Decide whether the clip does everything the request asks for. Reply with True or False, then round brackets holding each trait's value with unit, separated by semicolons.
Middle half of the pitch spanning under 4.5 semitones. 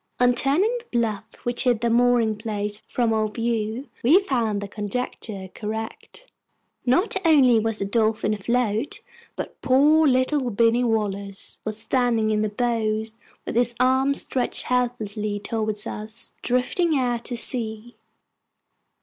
True (2.7 semitones)